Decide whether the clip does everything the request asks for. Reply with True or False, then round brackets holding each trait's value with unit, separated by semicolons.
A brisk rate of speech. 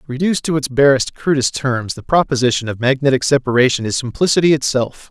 False (165 wpm)